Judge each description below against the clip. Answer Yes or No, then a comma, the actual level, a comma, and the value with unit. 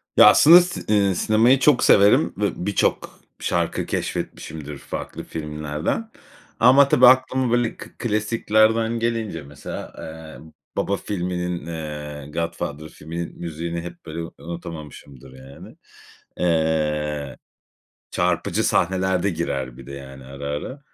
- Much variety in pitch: Yes, wide, 6.2 semitones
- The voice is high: No, very low, 85 Hz